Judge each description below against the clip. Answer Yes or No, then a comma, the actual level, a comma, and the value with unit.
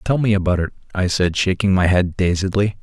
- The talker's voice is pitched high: No, very low, 95 Hz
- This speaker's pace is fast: Yes, fast, 215 wpm